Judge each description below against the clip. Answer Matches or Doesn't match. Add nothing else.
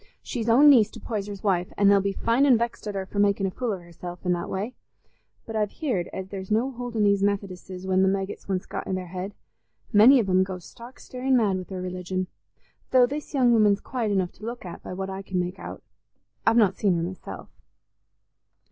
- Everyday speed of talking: Doesn't match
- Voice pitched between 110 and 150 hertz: Doesn't match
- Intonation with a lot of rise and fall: Doesn't match